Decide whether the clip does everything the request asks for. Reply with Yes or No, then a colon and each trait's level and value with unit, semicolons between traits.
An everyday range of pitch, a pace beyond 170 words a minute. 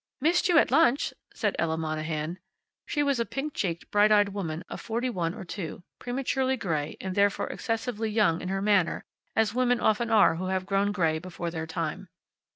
No: wide, 5.8 semitones; average, 190 wpm